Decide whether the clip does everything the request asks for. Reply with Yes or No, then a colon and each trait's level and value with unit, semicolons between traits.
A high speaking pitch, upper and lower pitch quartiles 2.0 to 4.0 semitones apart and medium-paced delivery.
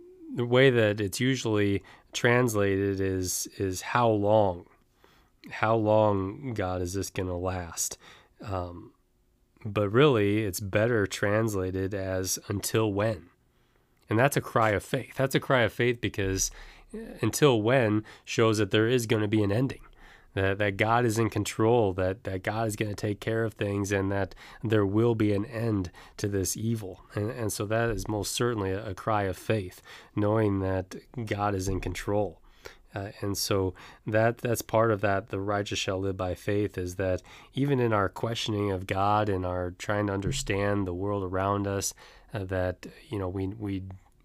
No: low, 105 Hz; average, 2.7 semitones; average, 175 wpm